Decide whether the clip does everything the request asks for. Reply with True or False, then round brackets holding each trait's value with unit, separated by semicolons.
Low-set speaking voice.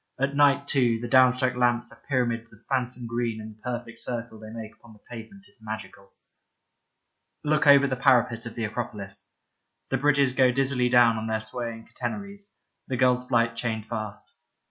True (120 Hz)